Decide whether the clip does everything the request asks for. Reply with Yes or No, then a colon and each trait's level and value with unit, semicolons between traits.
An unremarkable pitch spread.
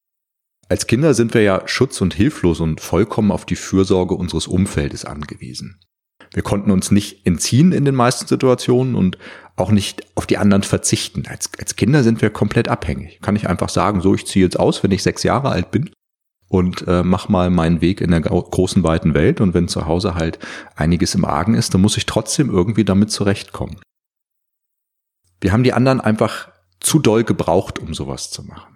Yes: average, 3.9 semitones